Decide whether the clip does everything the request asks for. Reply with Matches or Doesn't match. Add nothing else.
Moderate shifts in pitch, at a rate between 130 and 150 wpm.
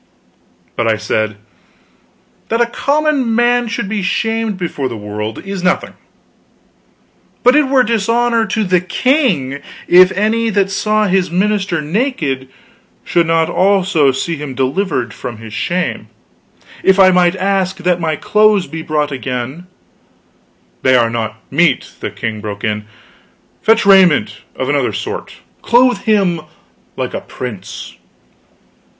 Doesn't match